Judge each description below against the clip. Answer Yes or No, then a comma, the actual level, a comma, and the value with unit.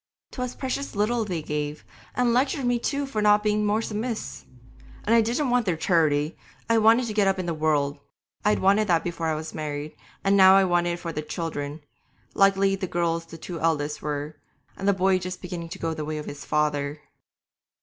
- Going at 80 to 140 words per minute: No, fast, 205 wpm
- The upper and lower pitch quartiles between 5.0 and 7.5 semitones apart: Yes, wide, 5.4 semitones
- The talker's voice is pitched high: No, medium, 180 Hz